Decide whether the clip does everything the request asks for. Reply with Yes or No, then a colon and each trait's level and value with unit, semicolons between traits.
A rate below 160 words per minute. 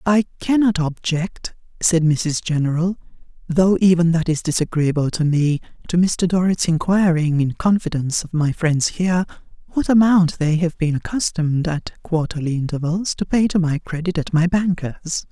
Yes: average, 150 wpm